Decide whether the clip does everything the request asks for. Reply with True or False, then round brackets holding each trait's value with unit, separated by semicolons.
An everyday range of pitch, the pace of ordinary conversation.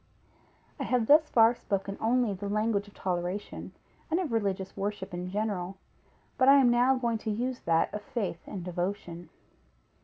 True (4.2 semitones; 165 wpm)